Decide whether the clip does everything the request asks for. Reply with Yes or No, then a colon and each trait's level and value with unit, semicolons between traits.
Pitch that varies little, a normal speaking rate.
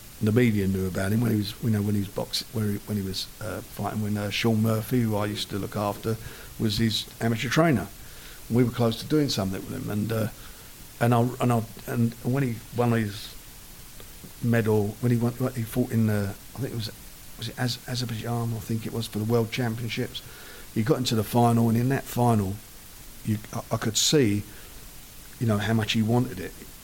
No: narrow, 2.2 semitones; fast, 220 wpm